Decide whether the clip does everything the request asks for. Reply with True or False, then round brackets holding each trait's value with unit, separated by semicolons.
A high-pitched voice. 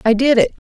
True (235 Hz)